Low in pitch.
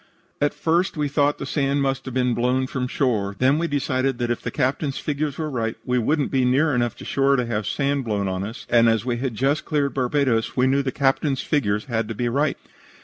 Yes: low, 130 Hz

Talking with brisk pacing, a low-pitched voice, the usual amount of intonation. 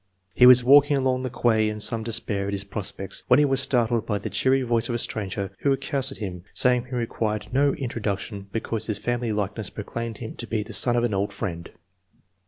Yes: fast, 235 wpm; low, 115 Hz; average, 3.3 semitones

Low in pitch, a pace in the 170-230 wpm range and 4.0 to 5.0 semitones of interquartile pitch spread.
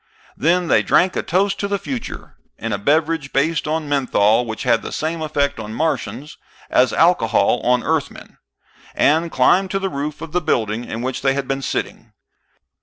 No: medium, 150 Hz; average, 180 wpm; average, 4.6 semitones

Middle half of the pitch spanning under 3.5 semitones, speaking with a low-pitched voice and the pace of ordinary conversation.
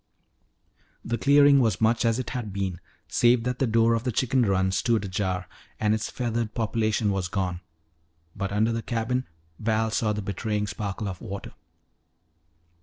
Yes: average, 2.9 semitones; low, 110 Hz; average, 165 wpm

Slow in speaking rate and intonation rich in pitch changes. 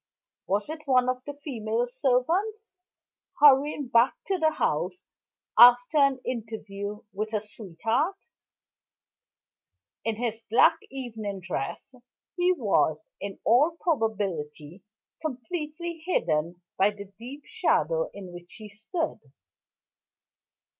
Yes: slow, 110 wpm; wide, 6.5 semitones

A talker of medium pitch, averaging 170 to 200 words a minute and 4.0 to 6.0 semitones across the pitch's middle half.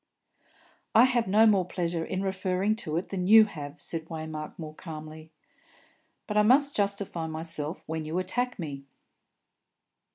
No: medium, 180 Hz; average, 150 wpm; average, 4.7 semitones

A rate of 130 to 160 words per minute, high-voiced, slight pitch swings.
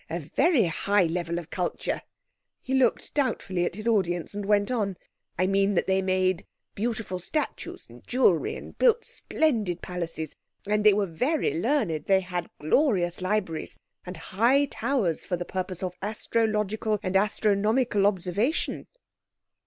No: average, 145 wpm; high, 195 Hz; average, 4.0 semitones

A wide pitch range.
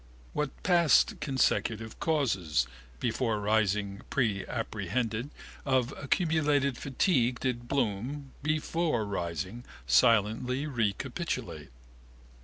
No: average, 5.0 semitones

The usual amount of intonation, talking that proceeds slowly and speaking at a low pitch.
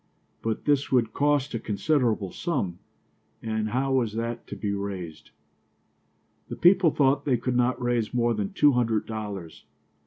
No: average, 4.0 semitones; average, 155 wpm; low, 115 Hz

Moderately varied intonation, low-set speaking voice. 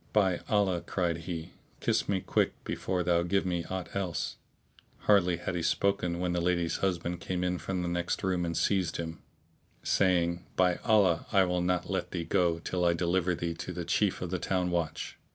No: narrow, 1.5 semitones; very low, 90 Hz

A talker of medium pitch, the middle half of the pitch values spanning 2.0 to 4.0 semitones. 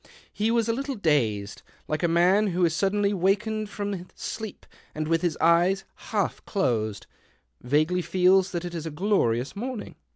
No: medium, 180 Hz; average, 4.4 semitones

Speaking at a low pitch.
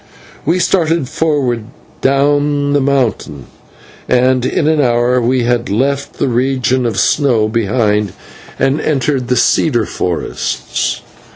Yes: low, 130 Hz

